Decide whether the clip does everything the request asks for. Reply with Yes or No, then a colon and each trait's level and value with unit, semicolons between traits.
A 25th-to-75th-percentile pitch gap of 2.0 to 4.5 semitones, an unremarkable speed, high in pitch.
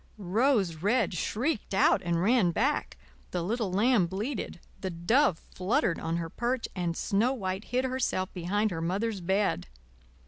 No: average, 5.2 semitones; average, 150 wpm; high, 200 Hz